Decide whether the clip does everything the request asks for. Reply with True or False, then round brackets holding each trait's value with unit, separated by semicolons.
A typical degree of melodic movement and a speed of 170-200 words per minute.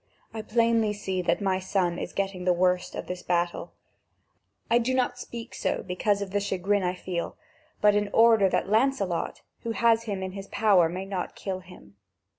True (3.3 semitones; 190 wpm)